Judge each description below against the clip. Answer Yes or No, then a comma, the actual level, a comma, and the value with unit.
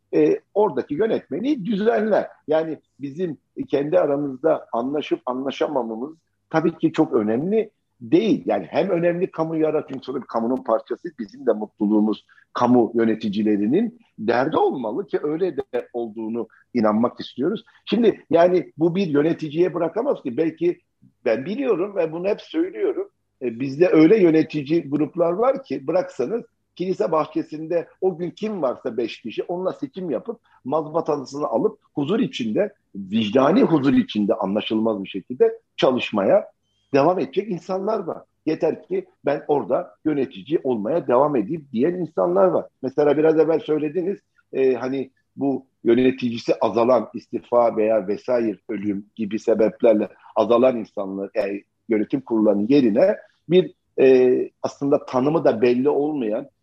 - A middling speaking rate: Yes, average, 125 wpm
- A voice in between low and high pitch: Yes, medium, 155 Hz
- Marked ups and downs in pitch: Yes, wide, 7.3 semitones